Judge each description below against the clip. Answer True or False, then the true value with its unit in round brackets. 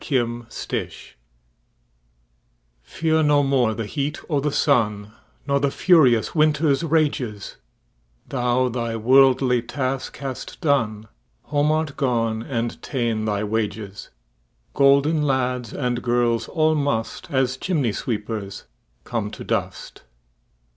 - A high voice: False (125 Hz)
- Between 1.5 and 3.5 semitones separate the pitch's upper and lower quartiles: False (4.2 semitones)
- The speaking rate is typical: False (100 wpm)